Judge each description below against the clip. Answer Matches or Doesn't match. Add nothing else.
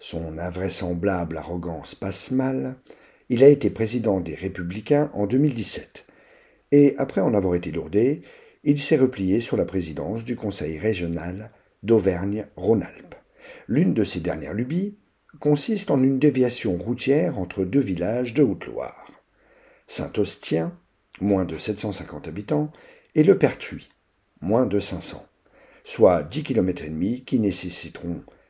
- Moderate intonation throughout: Doesn't match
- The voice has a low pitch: Matches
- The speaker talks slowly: Matches